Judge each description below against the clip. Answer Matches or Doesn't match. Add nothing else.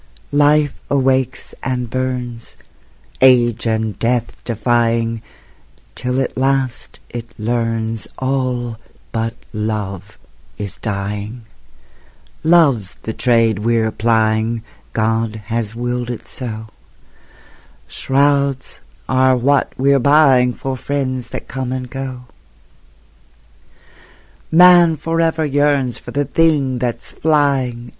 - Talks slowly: Matches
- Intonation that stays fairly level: Doesn't match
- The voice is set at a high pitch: Doesn't match